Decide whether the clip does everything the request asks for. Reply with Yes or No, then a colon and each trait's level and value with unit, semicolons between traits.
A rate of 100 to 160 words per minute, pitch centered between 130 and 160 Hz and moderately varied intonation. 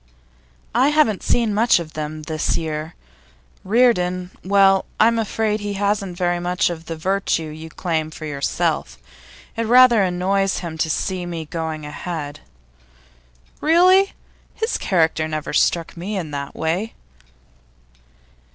No: slow, 135 wpm; medium, 180 Hz; average, 4.7 semitones